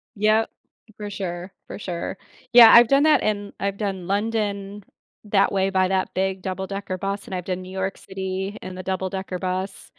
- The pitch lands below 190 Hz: No, high, 195 Hz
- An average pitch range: No, narrow, 1.5 semitones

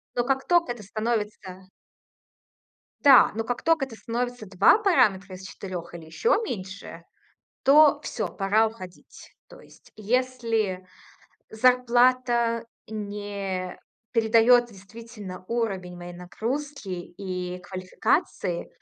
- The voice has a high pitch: Yes, high, 220 Hz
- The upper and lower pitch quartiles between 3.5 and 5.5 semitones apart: Yes, average, 4.7 semitones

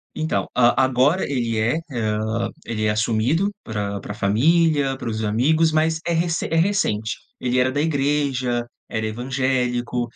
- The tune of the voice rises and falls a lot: Yes, wide, 5.7 semitones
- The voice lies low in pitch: Yes, low, 125 Hz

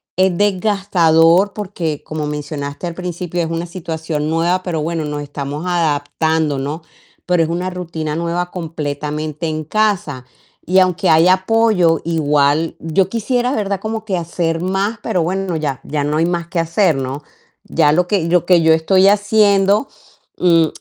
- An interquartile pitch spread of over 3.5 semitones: No, average, 3.2 semitones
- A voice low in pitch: No, medium, 170 Hz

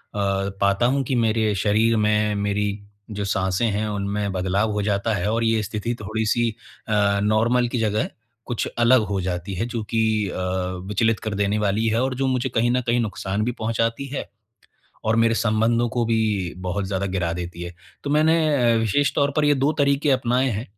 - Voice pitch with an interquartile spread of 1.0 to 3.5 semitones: Yes, average, 2.9 semitones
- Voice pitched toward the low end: Yes, low, 110 Hz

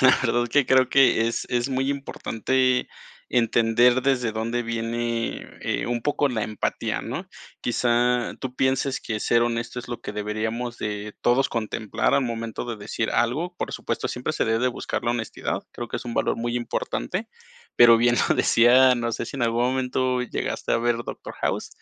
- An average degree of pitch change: No, narrow, 1.8 semitones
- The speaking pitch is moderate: No, low, 120 Hz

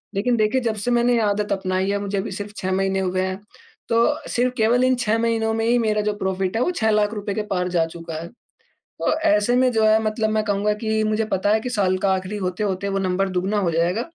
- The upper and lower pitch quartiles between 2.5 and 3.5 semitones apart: Yes, average, 2.8 semitones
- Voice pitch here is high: Yes, high, 210 Hz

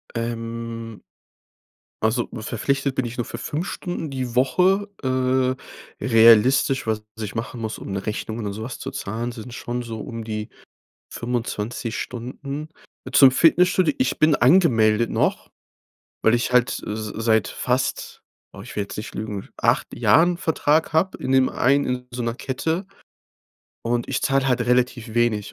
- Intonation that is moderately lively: Yes, average, 3.0 semitones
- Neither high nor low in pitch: No, low, 120 Hz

